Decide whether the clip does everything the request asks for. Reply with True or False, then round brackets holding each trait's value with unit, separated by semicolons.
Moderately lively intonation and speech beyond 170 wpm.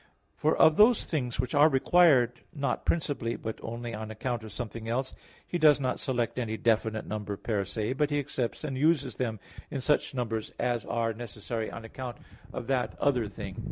True (3.7 semitones; 190 wpm)